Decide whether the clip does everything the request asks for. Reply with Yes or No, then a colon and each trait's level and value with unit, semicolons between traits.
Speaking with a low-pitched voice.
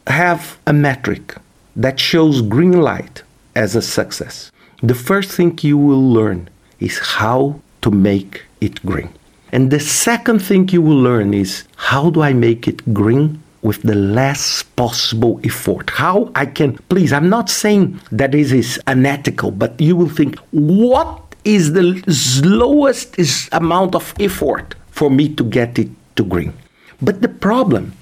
No: medium, 145 Hz